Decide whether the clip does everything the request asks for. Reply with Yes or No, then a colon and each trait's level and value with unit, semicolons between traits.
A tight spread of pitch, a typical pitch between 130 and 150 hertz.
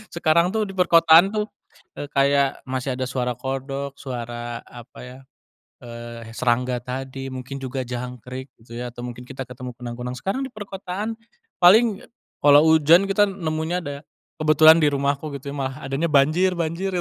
No: average, 4.9 semitones; medium, 140 Hz